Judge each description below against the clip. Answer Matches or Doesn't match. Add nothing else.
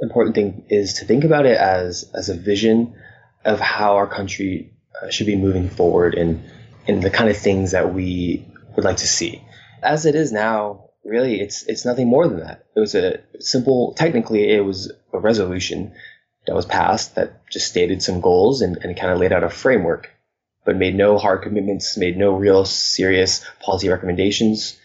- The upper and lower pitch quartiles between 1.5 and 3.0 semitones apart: Matches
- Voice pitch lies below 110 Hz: Matches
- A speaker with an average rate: Matches